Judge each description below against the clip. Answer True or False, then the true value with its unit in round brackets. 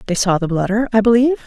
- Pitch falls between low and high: False (215 Hz)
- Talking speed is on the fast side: True (245 wpm)